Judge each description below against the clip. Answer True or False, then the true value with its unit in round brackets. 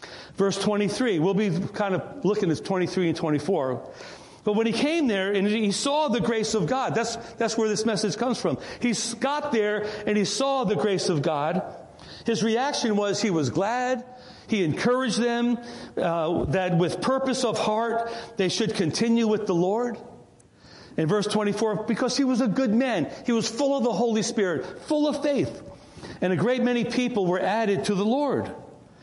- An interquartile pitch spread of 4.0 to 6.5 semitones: False (3.5 semitones)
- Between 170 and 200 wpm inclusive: True (195 wpm)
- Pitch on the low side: False (220 Hz)